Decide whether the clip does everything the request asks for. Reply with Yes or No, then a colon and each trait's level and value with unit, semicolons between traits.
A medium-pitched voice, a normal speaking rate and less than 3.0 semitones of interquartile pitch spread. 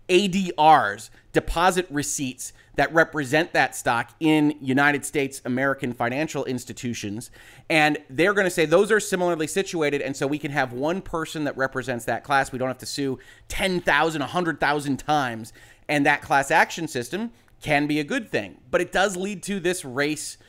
No: medium, 145 Hz; average, 170 wpm; average, 3.9 semitones